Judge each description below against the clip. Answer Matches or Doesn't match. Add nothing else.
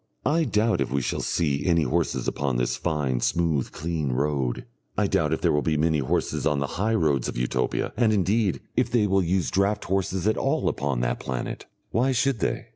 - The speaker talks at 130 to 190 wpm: Doesn't match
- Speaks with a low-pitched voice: Matches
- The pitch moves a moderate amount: Doesn't match